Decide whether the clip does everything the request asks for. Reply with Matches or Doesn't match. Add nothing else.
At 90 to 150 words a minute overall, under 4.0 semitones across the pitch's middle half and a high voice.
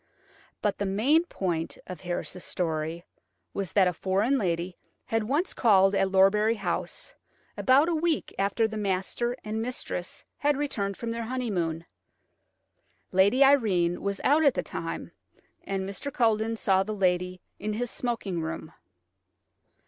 Doesn't match